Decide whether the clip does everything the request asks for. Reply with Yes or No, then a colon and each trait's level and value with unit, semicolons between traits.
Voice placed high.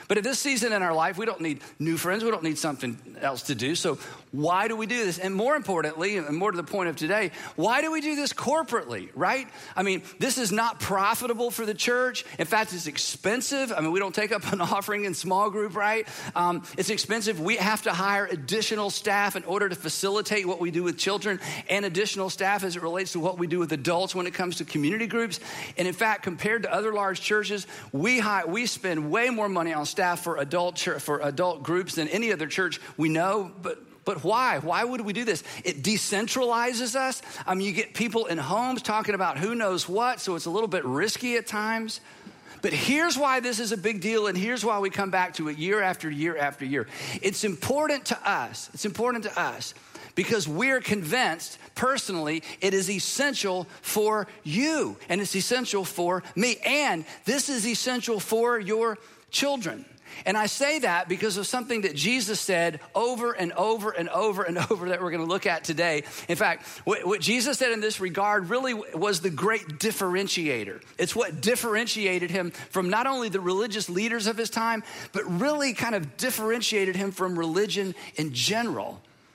Yes: high, 200 Hz